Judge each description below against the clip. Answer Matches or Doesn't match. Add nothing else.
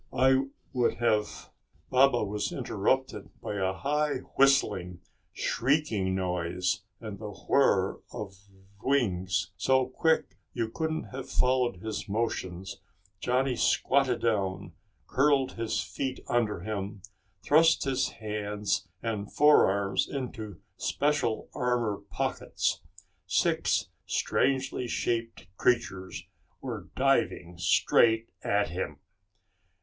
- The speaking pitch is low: Matches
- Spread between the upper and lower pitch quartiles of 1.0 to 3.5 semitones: Doesn't match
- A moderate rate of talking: Doesn't match